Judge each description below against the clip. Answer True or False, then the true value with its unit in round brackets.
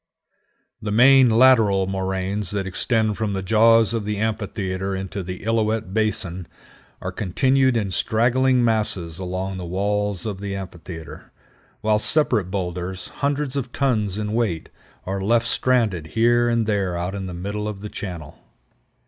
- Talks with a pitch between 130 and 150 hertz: False (105 Hz)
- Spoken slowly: False (150 wpm)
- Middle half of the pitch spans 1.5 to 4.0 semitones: True (3.3 semitones)